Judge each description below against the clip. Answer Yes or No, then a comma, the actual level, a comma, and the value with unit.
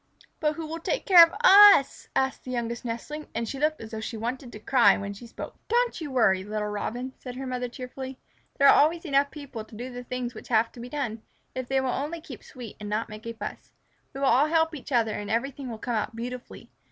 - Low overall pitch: No, very high, 250 Hz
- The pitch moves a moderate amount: Yes, average, 3.8 semitones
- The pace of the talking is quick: Yes, fast, 245 wpm